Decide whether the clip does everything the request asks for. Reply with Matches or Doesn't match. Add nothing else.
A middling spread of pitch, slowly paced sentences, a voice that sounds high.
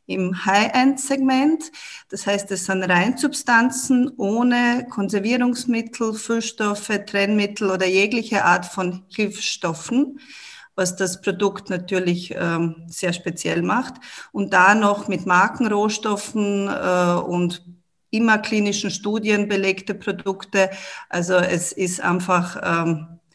Matches